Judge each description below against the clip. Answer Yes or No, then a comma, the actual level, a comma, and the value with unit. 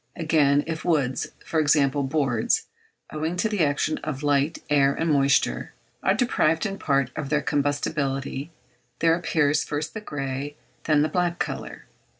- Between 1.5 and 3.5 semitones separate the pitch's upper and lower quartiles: Yes, narrow, 2.6 semitones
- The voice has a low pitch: No, medium, 150 Hz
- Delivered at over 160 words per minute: No, average, 150 wpm